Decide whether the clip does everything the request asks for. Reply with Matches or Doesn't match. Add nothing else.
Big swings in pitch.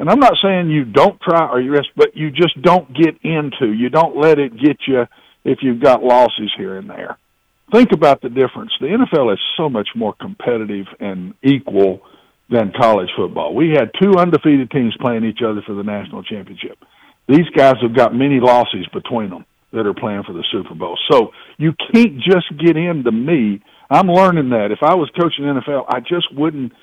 Matches